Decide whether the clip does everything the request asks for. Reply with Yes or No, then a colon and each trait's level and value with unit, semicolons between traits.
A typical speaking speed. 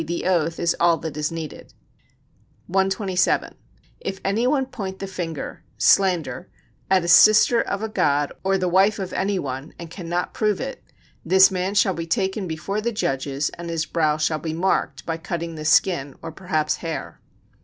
Yes: average, 180 wpm